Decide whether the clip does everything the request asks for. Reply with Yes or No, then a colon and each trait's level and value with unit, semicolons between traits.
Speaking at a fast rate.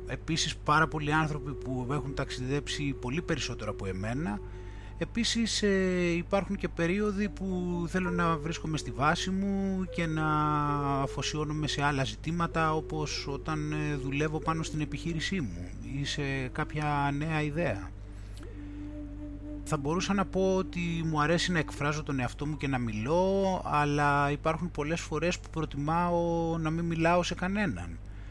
No: average, 140 wpm